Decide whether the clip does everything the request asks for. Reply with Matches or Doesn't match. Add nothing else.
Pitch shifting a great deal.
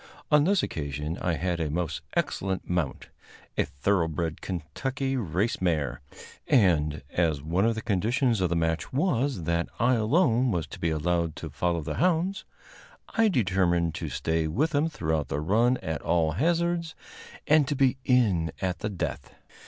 Matches